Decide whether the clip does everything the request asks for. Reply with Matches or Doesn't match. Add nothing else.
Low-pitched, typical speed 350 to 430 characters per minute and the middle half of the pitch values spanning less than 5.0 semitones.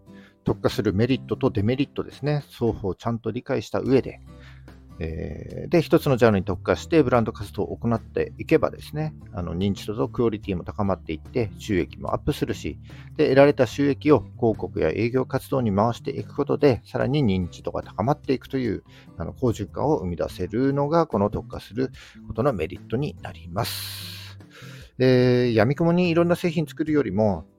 Doesn't match